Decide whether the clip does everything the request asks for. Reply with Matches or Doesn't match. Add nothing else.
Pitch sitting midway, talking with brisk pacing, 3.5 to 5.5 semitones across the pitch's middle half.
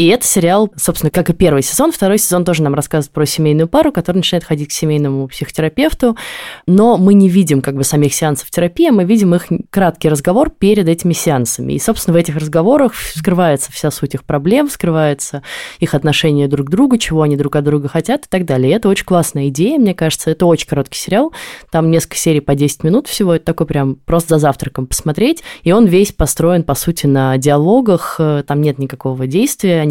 Matches